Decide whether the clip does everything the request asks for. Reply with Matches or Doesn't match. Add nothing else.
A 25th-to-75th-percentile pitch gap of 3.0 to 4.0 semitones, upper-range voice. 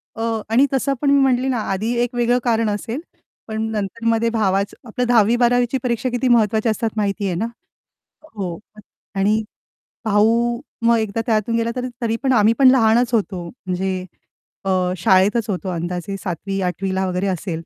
Matches